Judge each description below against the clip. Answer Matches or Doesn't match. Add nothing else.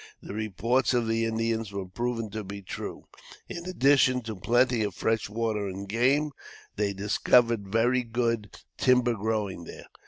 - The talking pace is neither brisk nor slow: Matches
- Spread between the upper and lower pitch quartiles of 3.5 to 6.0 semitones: Doesn't match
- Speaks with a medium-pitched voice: Doesn't match